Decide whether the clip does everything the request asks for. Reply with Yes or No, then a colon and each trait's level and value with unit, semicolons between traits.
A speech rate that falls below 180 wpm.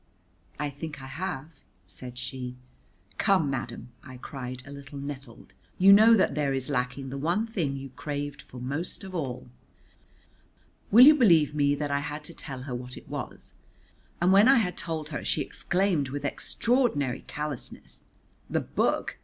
Yes: average, 170 wpm